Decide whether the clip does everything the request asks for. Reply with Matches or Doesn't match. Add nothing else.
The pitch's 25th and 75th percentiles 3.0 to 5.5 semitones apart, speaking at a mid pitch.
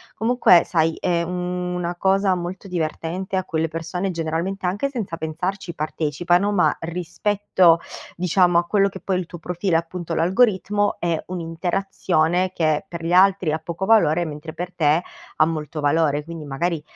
Doesn't match